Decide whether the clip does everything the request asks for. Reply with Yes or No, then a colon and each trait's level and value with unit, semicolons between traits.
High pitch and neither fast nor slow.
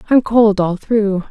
Yes: high, 210 Hz; average, 185 wpm